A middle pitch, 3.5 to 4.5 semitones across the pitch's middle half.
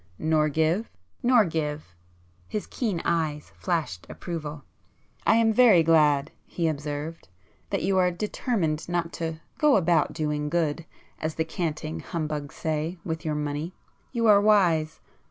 No: medium, 160 Hz; average, 3.1 semitones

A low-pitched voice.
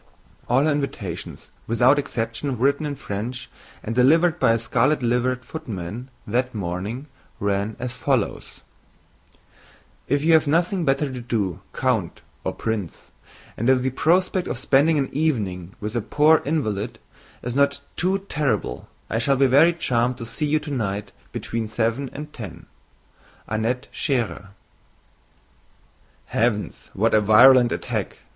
Yes: low, 125 Hz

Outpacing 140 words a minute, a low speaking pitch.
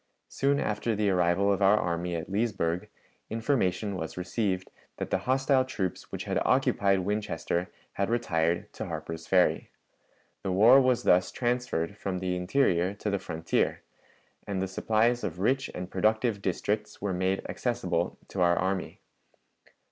Yes: average, 150 wpm; very low, 95 Hz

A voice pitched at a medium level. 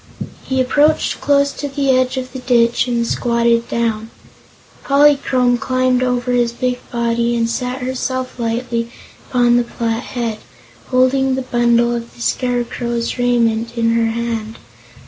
No: high, 245 Hz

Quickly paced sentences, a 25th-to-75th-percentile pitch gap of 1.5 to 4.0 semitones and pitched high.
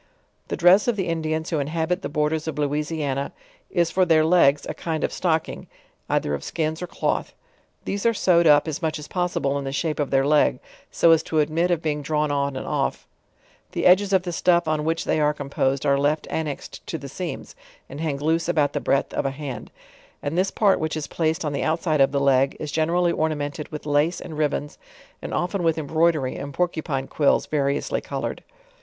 No: fast, 215 wpm; narrow, 2.6 semitones; medium, 155 Hz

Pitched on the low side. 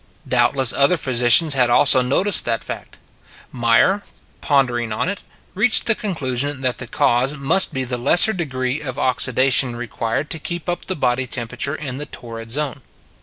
Yes: low, 130 Hz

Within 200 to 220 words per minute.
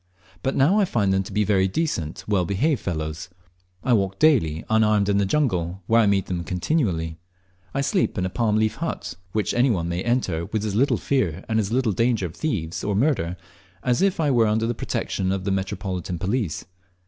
Yes: fast, 205 wpm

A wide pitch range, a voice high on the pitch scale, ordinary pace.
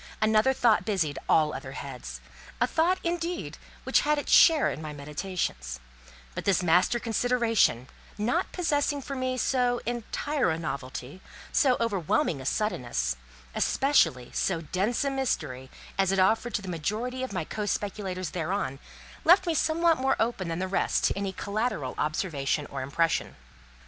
Yes: wide, 8.5 semitones; high, 200 Hz; average, 155 wpm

